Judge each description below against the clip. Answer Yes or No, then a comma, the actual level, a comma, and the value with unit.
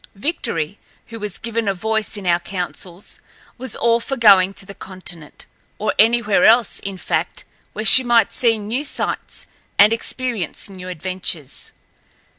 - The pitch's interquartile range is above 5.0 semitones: No, average, 3.9 semitones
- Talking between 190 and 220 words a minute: No, average, 150 wpm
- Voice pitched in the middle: No, high, 205 Hz